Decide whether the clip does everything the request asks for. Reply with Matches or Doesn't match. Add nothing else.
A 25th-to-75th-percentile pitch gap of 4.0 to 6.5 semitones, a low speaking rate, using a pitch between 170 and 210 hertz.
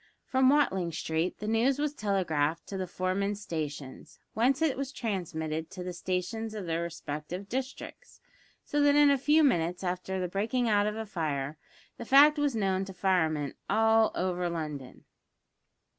Doesn't match